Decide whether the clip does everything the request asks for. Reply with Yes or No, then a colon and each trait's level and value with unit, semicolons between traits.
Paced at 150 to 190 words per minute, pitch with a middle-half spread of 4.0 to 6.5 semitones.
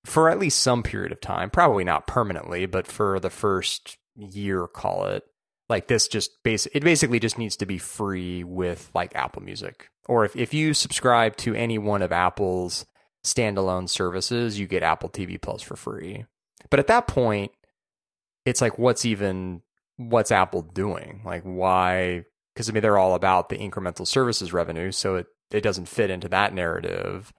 Yes: average, 180 wpm; average, 4.5 semitones